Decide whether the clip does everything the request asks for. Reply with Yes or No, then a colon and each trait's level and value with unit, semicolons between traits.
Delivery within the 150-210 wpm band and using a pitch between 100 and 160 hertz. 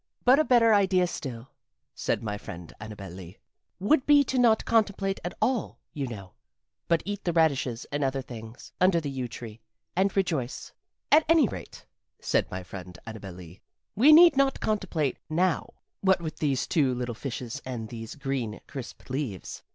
Yes: average, 170 wpm; medium, 140 Hz